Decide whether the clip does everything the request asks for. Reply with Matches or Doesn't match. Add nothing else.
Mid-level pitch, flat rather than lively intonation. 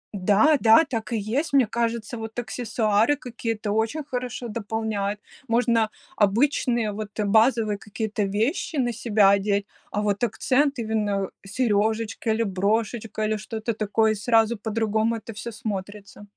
Doesn't match